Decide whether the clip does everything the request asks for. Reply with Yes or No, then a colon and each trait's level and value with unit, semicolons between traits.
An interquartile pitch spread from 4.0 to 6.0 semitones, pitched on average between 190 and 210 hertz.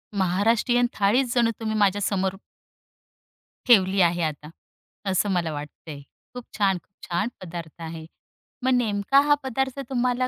Yes: wide, 5.6 semitones; high, 200 Hz